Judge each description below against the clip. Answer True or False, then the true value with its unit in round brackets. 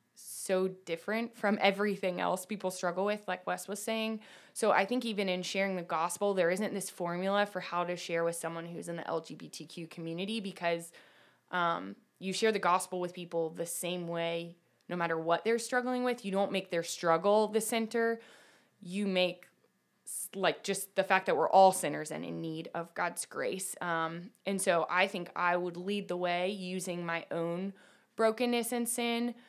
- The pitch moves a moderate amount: True (3.1 semitones)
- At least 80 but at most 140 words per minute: False (185 wpm)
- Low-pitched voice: False (185 Hz)